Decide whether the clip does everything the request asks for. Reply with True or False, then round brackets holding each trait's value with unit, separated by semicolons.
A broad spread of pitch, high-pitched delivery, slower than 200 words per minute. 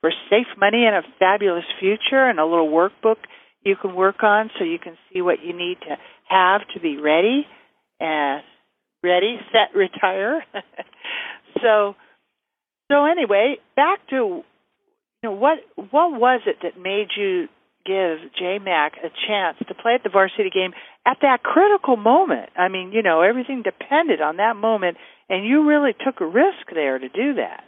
True (8.2 semitones; 220 Hz; 170 wpm)